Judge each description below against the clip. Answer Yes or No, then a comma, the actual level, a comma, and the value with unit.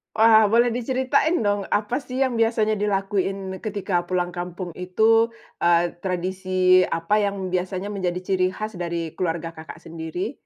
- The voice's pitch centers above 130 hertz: Yes, high, 190 Hz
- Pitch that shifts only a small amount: No, average, 3.3 semitones